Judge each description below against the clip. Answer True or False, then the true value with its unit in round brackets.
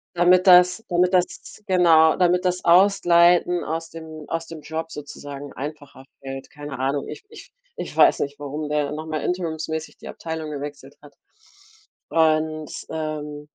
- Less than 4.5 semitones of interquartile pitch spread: True (2.9 semitones)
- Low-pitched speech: False (160 Hz)